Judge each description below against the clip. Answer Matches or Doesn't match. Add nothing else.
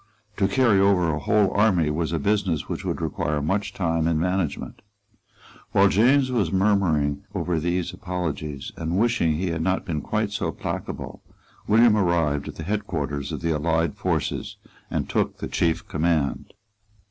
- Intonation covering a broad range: Doesn't match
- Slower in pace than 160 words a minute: Doesn't match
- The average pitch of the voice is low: Matches